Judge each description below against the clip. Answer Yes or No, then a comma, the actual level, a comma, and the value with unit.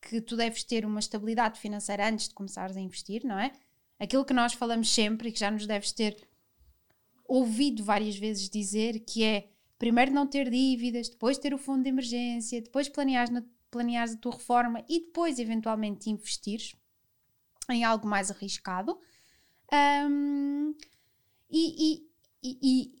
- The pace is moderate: Yes, average, 155 wpm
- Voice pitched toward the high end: Yes, high, 235 Hz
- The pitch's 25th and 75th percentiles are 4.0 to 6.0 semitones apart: No, average, 3.5 semitones